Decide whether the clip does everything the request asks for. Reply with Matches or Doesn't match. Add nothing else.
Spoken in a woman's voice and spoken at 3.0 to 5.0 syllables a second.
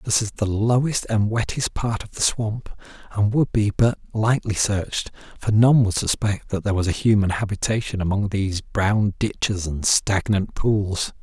Doesn't match